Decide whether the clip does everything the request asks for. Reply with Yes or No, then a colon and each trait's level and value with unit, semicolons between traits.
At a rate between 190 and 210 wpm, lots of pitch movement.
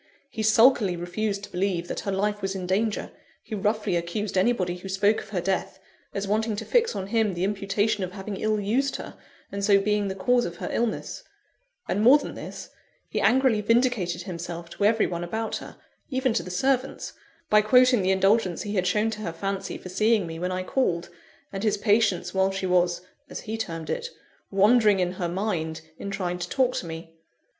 No: fast, 205 wpm; average, 3.3 semitones